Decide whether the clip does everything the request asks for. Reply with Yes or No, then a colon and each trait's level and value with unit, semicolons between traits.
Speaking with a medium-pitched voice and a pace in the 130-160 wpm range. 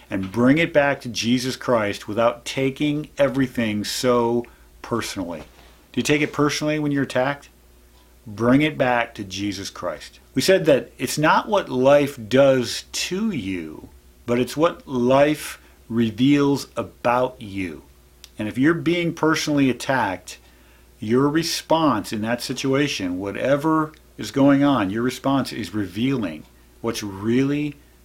No: low, 125 Hz; slow, 135 wpm